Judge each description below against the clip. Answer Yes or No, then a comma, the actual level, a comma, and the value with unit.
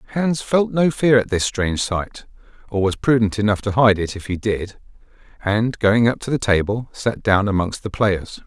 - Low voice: Yes, low, 110 Hz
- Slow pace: No, fast, 205 wpm